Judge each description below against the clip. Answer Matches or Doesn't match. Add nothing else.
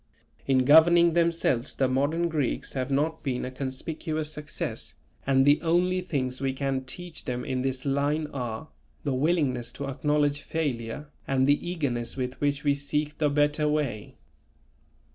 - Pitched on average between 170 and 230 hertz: Doesn't match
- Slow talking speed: Doesn't match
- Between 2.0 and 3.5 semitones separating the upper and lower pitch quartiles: Matches